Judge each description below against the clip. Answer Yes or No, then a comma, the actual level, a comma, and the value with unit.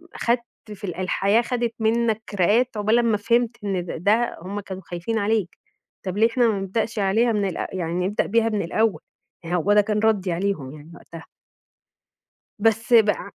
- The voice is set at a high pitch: Yes, high, 210 Hz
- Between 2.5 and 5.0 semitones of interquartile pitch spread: Yes, average, 3.3 semitones